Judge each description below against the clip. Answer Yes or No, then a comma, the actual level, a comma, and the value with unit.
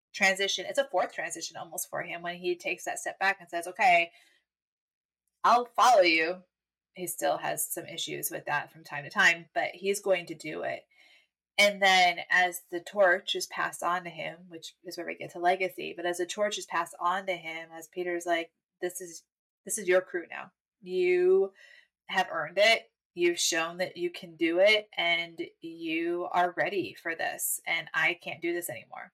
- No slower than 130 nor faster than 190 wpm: No, average, 200 wpm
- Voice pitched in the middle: Yes, medium, 180 Hz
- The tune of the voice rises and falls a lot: Yes, wide, 5.7 semitones